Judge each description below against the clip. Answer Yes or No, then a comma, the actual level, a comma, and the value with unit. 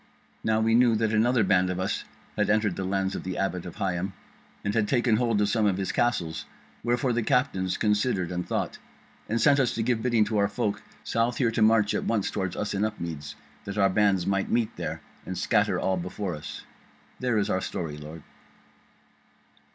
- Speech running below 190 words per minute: No, fast, 205 wpm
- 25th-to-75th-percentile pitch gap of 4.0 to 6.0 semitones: No, average, 3.4 semitones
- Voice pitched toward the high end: No, low, 105 Hz